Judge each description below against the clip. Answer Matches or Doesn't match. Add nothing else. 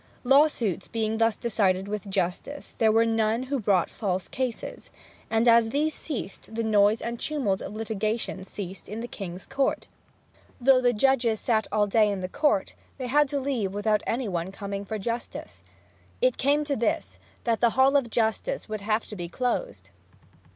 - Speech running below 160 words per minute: Doesn't match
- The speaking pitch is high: Matches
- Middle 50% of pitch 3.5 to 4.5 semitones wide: Matches